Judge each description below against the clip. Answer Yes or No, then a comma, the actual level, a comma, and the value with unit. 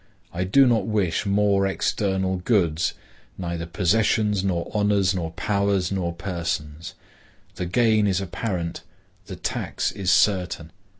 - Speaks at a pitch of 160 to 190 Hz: No, very low, 95 Hz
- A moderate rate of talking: No, slow, 120 wpm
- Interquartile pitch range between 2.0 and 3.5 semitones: Yes, average, 2.9 semitones